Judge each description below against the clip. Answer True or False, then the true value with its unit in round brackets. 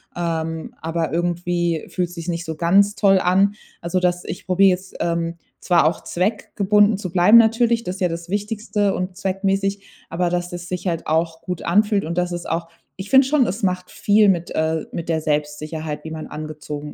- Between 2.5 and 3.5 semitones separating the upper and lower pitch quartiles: True (2.9 semitones)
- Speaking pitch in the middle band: True (175 Hz)